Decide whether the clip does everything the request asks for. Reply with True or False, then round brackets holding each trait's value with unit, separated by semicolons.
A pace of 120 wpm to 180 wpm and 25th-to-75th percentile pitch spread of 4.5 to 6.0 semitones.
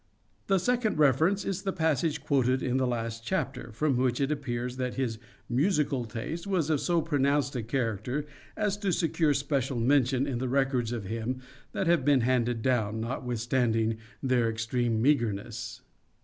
False (165 wpm; 4.1 semitones)